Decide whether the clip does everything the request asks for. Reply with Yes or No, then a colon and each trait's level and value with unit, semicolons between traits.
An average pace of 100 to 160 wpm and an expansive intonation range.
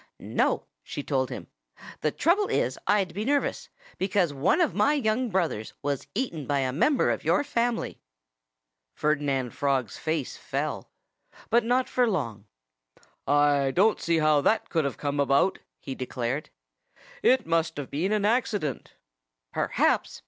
Yes: average, 150 wpm; wide, 7.7 semitones